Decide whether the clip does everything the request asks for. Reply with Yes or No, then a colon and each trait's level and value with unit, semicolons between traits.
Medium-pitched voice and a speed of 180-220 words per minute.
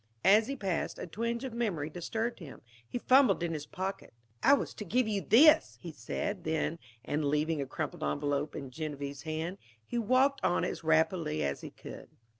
Yes: medium, 175 Hz; average, 190 wpm